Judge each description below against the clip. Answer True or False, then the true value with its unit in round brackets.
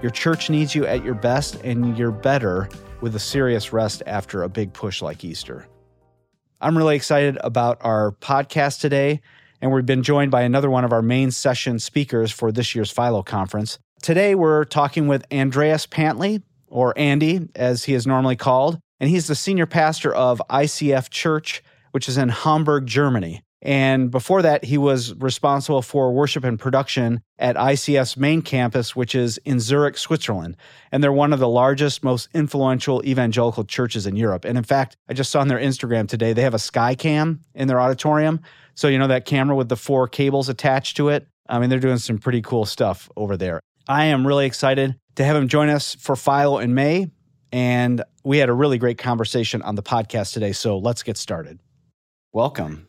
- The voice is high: False (130 Hz)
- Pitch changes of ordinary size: True (3.1 semitones)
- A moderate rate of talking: True (190 wpm)